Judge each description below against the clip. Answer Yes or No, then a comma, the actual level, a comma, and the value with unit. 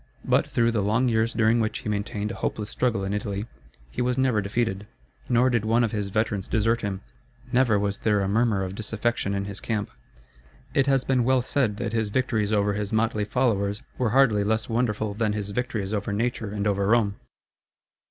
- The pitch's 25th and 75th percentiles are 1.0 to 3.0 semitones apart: Yes, narrow, 2.5 semitones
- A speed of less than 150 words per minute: No, average, 200 wpm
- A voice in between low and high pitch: No, low, 110 Hz